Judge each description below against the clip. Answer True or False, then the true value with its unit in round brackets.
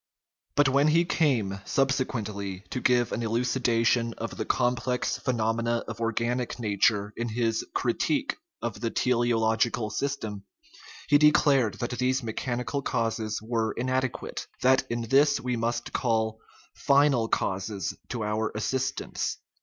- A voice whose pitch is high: False (120 Hz)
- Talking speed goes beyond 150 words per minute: False (140 wpm)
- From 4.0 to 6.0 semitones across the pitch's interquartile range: False (2.6 semitones)